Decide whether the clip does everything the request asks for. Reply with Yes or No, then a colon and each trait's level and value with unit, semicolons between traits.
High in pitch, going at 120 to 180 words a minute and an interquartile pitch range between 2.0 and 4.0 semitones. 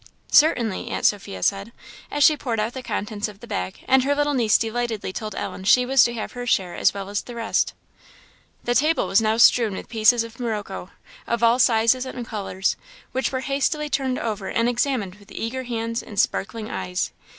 No: high, 230 Hz; average, 200 wpm; average, 3.4 semitones